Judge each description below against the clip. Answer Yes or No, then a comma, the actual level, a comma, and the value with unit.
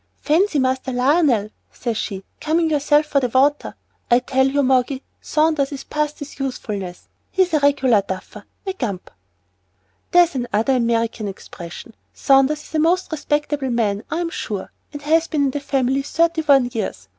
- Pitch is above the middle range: Yes, very high, 275 Hz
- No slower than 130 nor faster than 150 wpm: No, average, 160 wpm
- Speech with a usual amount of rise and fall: Yes, average, 3.9 semitones